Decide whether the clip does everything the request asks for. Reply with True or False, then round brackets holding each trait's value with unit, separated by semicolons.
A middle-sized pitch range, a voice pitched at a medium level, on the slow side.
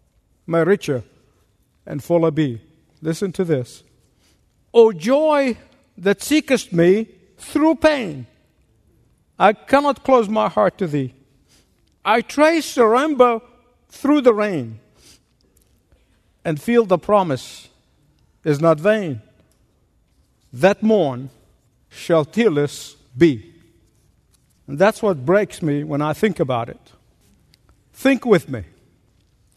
False (8.6 semitones; 170 Hz; 110 wpm)